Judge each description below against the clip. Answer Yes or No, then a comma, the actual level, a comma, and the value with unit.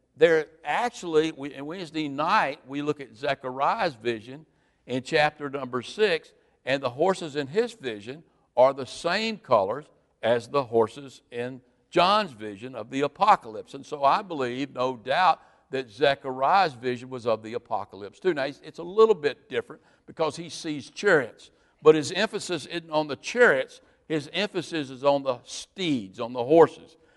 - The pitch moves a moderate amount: No, wide, 6.6 semitones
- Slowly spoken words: No, average, 165 wpm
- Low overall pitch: No, medium, 150 Hz